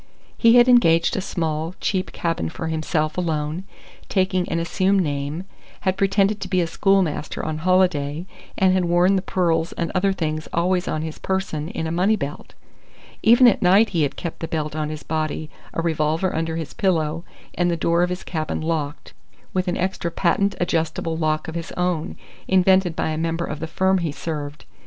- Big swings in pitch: No, average, 3.1 semitones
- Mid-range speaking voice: Yes, medium, 170 Hz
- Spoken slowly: No, average, 190 wpm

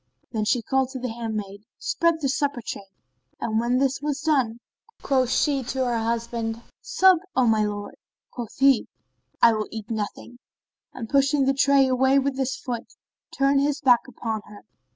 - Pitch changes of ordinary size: Yes, average, 3.4 semitones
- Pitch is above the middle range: Yes, very high, 255 Hz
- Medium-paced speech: Yes, average, 175 wpm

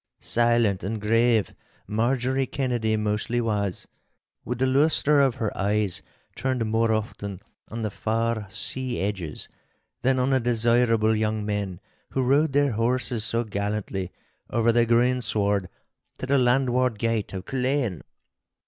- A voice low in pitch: Yes, low, 115 Hz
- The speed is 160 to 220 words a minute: No, slow, 135 wpm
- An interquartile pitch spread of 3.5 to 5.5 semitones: No, average, 3.1 semitones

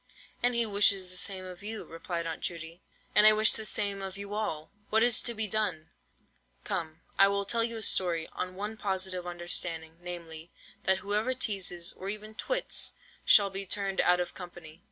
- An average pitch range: Yes, average, 3.4 semitones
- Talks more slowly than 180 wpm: No, average, 195 wpm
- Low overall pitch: No, high, 190 Hz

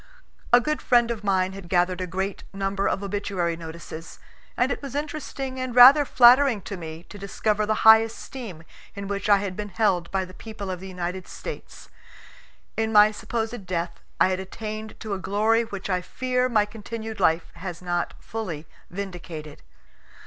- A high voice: Yes, high, 200 Hz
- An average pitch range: Yes, average, 3.5 semitones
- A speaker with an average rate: Yes, average, 180 wpm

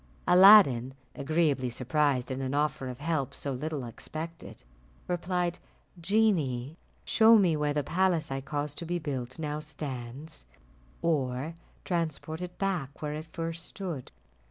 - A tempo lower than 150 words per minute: Yes, slow, 135 wpm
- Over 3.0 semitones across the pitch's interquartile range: Yes, average, 4.0 semitones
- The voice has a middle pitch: Yes, medium, 150 Hz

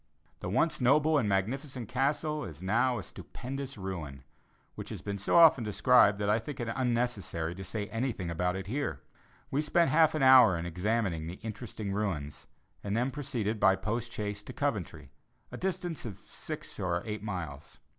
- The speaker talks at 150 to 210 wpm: Yes, average, 175 wpm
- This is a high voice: No, low, 110 Hz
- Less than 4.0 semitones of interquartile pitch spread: No, wide, 5.6 semitones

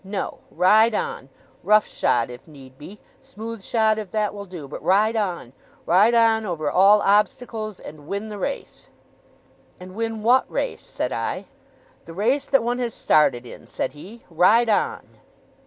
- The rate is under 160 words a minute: No, average, 165 wpm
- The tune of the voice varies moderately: Yes, average, 4.2 semitones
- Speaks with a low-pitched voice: No, high, 210 Hz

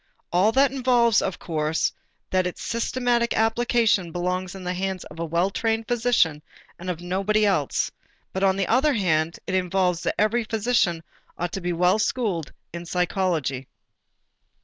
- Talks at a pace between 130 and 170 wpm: Yes, average, 160 wpm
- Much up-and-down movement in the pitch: No, average, 4.3 semitones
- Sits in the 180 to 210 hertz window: Yes, high, 190 Hz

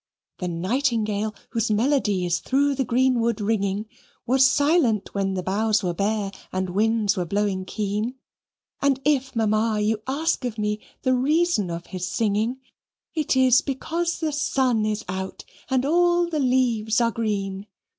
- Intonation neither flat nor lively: Yes, average, 4.6 semitones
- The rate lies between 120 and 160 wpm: Yes, average, 155 wpm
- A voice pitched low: No, high, 225 Hz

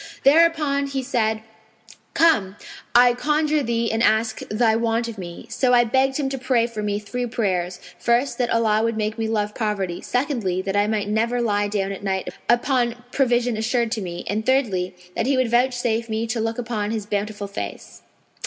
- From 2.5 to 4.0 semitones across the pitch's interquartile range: Yes, average, 2.9 semitones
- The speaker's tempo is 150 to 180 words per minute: No, average, 190 wpm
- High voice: Yes, high, 230 Hz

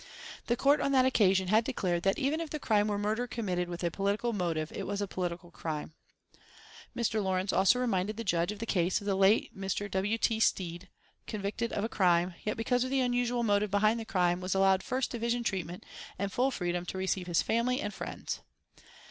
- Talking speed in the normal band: No, fast, 210 wpm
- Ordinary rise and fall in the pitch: Yes, average, 4.1 semitones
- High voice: Yes, high, 205 Hz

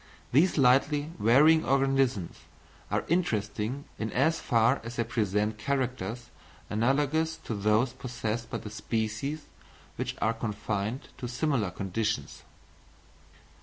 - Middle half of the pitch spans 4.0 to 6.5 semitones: Yes, average, 4.3 semitones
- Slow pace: Yes, slow, 115 wpm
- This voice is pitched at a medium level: No, low, 120 Hz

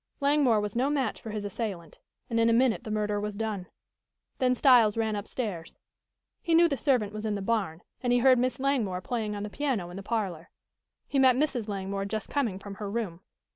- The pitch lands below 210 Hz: No, high, 220 Hz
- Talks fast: Yes, fast, 210 wpm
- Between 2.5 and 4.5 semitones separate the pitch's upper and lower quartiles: Yes, average, 3.9 semitones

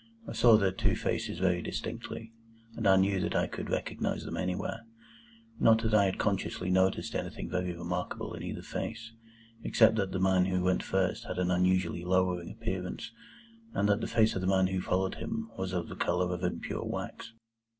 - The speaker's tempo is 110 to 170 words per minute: No, average, 190 wpm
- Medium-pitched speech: No, very low, 95 Hz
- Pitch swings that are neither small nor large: No, narrow, 1.8 semitones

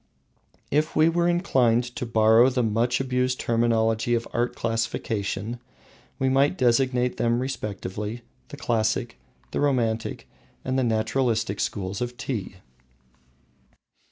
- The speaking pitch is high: No, low, 120 Hz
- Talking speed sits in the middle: No, slow, 120 wpm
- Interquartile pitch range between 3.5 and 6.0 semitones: No, narrow, 2.5 semitones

